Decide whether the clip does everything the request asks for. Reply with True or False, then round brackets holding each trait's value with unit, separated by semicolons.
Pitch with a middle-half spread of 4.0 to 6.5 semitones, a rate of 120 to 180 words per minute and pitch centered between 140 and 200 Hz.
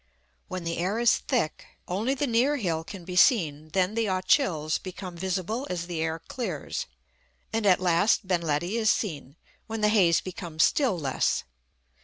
True (4.7 semitones; 170 wpm; 185 Hz)